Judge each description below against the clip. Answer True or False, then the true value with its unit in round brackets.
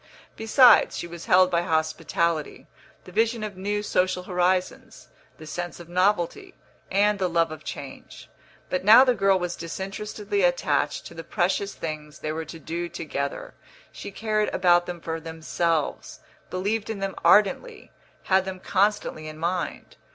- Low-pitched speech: False (185 Hz)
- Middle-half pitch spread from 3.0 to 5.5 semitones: True (3.7 semitones)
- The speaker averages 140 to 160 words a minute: True (155 wpm)